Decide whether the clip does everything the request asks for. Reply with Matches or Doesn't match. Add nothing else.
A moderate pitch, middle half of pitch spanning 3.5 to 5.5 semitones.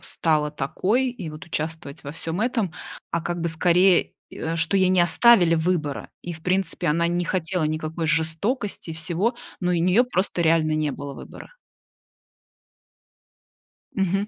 Doesn't match